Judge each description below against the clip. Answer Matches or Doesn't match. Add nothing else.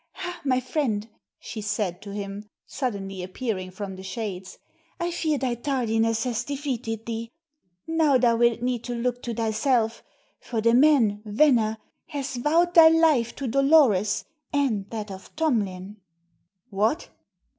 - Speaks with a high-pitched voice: Matches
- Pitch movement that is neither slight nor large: Matches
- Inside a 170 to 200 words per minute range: Doesn't match